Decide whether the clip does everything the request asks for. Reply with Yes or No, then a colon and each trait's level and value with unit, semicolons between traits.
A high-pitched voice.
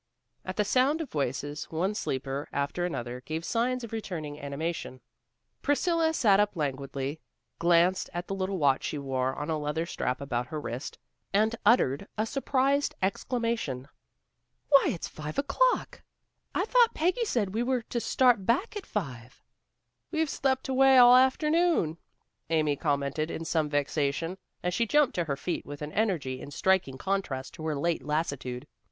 No: medium, 170 Hz